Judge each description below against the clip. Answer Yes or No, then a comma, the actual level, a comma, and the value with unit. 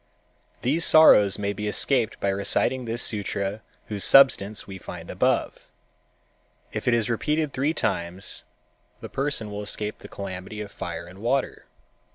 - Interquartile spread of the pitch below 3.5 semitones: No, average, 4.7 semitones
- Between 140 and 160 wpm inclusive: Yes, average, 150 wpm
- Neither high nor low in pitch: No, low, 105 Hz